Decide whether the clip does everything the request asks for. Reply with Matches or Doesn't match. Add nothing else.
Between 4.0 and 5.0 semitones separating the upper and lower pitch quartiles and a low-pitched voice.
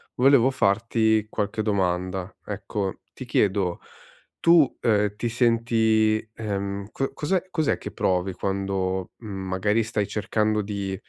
Doesn't match